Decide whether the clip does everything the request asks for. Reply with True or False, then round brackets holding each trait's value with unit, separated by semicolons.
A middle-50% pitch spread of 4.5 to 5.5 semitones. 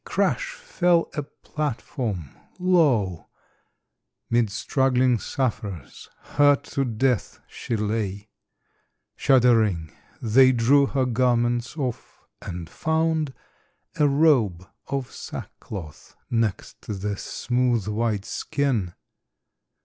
True (4.9 semitones)